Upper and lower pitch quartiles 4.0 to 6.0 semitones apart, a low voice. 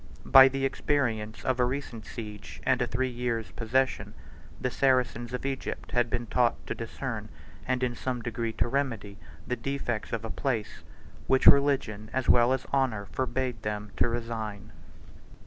No: average, 2.7 semitones; low, 120 Hz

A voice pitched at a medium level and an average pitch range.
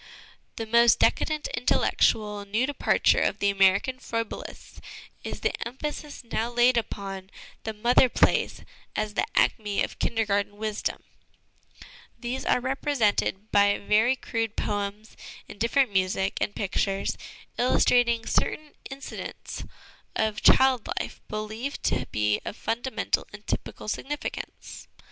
No: high, 220 Hz; average, 3.6 semitones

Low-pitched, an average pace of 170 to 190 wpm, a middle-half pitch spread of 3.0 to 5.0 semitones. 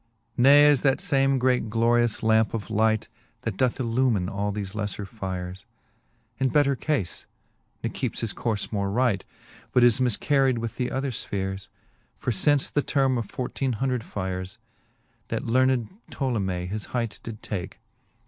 No: low, 115 Hz; average, 155 wpm; average, 4.3 semitones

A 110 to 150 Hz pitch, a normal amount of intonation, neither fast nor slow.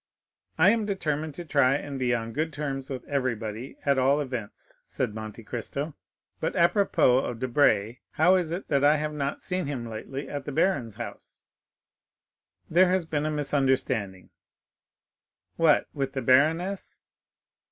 Yes: medium, 140 Hz; average, 3.8 semitones; average, 150 wpm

